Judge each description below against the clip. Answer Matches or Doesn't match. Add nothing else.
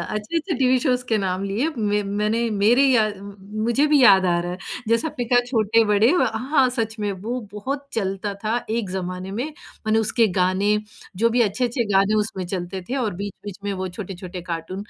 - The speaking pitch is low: Doesn't match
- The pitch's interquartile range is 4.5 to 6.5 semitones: Doesn't match